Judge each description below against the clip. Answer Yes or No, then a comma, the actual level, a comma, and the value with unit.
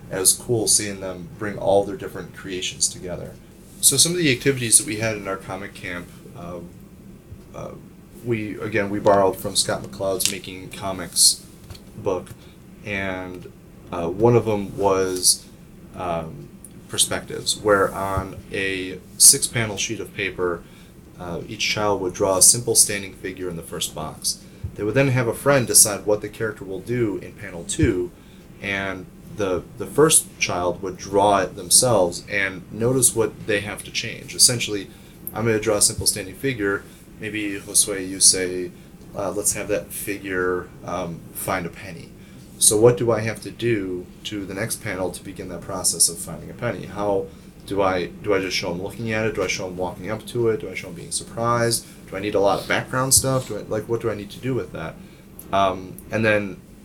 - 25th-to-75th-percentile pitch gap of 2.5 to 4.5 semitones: Yes, average, 3.0 semitones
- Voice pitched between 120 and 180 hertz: No, low, 100 Hz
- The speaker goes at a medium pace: Yes, average, 190 wpm